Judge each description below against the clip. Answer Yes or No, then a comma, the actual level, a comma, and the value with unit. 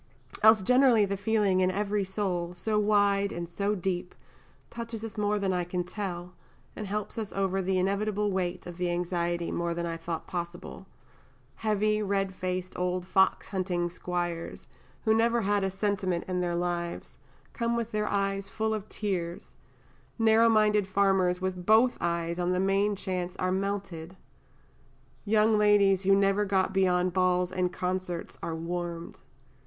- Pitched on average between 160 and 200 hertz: Yes, high, 190 Hz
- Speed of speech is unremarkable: Yes, average, 160 wpm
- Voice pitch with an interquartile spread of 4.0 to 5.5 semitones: No, average, 2.7 semitones